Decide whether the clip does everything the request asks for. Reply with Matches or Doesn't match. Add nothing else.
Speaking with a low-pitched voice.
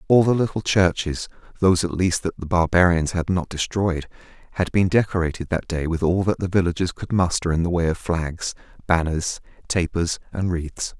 Matches